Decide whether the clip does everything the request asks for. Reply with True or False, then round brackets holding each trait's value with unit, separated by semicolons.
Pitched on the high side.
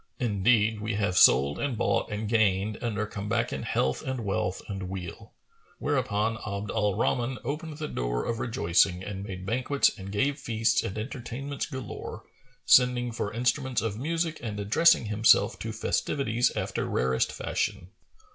False (110 Hz)